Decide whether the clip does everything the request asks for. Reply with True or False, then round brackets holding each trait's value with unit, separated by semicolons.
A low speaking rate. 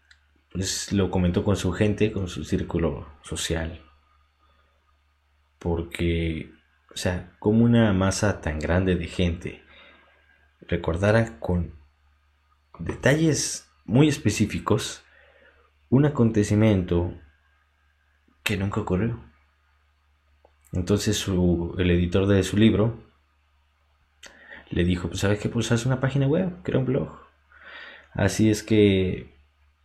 True (105 wpm)